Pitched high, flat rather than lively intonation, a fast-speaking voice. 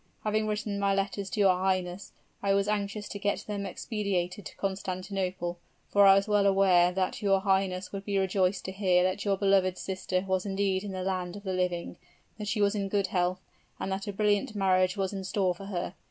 Yes: high, 195 Hz; narrow, 1.5 semitones; fast, 210 wpm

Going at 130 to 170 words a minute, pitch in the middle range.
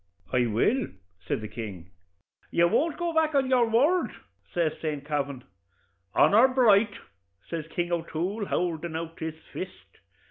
Yes: average, 140 wpm; medium, 175 Hz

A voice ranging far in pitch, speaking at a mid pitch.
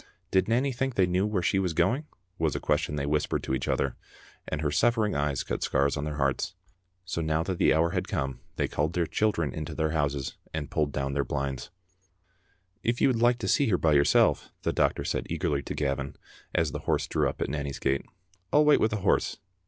No: wide, 5.7 semitones; very low, 80 Hz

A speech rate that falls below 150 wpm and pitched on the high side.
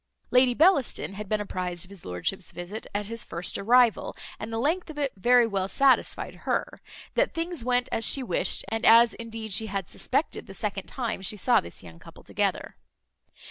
No: average, 190 wpm; high, 225 Hz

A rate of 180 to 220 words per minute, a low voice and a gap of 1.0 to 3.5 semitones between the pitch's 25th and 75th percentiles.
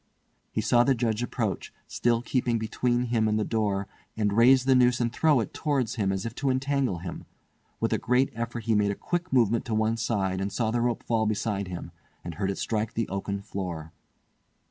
Yes: fast, 205 wpm; low, 115 Hz; average, 3.2 semitones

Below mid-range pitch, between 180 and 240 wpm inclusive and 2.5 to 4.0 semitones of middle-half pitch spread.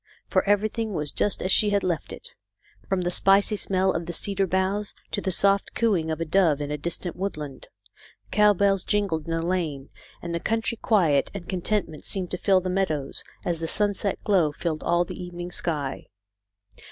No: medium, 185 Hz; average, 190 wpm; average, 3.3 semitones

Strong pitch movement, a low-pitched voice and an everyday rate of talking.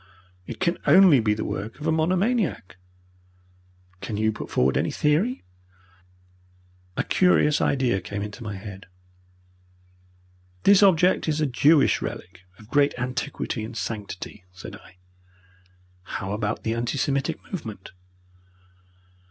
No: wide, 7.3 semitones; low, 125 Hz; slow, 125 wpm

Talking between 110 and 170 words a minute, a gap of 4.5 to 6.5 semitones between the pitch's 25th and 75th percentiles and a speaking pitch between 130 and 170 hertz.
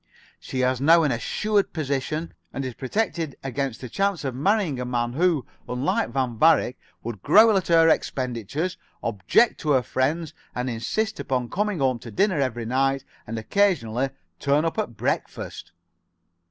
Yes: average, 160 wpm; average, 5.2 semitones; low, 135 Hz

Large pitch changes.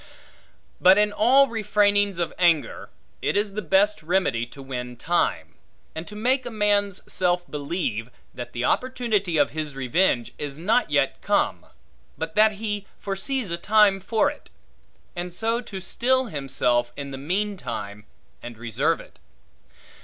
Yes: wide, 6.8 semitones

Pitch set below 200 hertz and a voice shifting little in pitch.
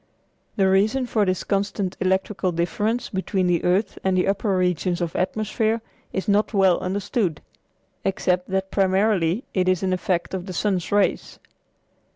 Yes: high, 190 Hz; narrow, 2.0 semitones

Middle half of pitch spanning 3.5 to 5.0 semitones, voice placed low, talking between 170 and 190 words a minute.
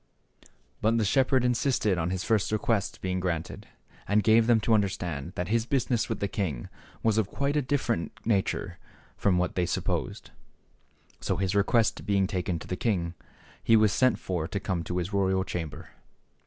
Yes: average, 3.9 semitones; low, 100 Hz; average, 180 wpm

